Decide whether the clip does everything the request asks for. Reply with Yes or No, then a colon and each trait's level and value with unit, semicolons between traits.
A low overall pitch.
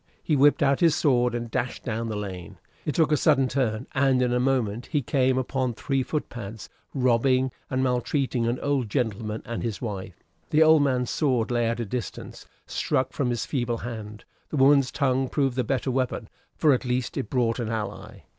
Yes: low, 125 Hz